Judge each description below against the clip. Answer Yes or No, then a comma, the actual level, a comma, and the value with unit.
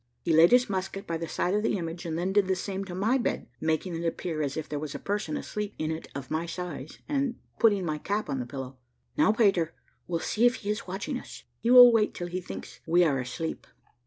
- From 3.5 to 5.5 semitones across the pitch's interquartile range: Yes, average, 4.6 semitones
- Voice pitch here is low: No, medium, 180 Hz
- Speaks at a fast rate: Yes, fast, 245 wpm